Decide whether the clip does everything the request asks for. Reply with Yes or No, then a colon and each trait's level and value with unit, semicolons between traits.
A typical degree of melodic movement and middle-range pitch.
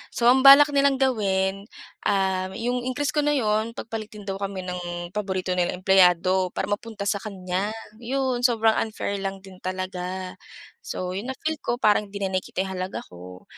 No: average, 4.3 semitones; high, 200 Hz